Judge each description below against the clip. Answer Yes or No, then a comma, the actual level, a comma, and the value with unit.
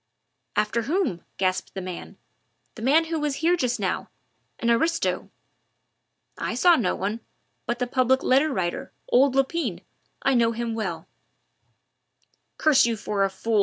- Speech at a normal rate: Yes, average, 155 wpm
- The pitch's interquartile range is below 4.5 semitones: No, average, 5.0 semitones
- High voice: Yes, high, 240 Hz